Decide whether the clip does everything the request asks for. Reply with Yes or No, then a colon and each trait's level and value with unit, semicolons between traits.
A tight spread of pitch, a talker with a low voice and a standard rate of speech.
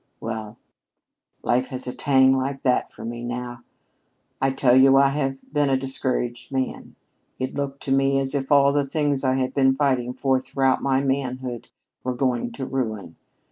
Yes: narrow, 1.5 semitones; low, 130 Hz; average, 180 wpm